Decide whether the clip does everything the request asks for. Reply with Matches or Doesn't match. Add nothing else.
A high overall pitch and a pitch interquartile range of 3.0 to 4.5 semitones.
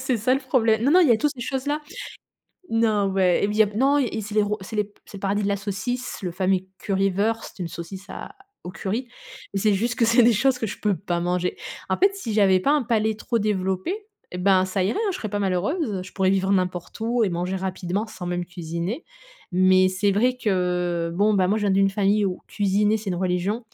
Matches